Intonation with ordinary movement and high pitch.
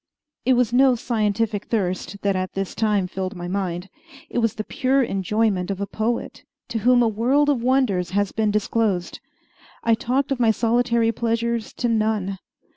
Yes: average, 3.3 semitones; high, 220 Hz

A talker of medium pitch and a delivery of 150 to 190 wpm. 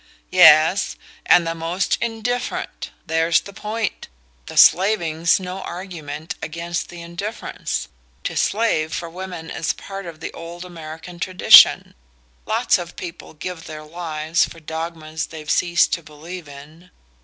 No: medium, 170 Hz; slow, 135 wpm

